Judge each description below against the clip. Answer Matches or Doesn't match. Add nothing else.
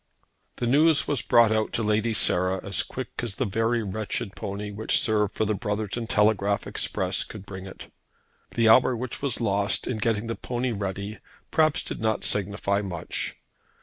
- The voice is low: Matches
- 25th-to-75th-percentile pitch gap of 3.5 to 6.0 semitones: Doesn't match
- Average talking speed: Matches